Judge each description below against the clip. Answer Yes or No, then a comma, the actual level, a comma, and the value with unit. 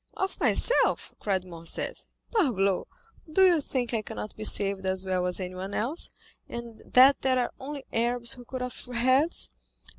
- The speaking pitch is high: Yes, high, 235 Hz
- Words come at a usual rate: Yes, average, 160 wpm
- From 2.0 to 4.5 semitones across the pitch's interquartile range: No, wide, 5.4 semitones